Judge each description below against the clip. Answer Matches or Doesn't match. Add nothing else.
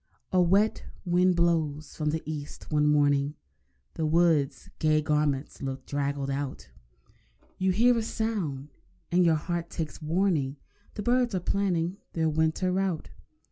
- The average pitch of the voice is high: Doesn't match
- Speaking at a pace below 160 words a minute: Matches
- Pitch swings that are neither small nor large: Matches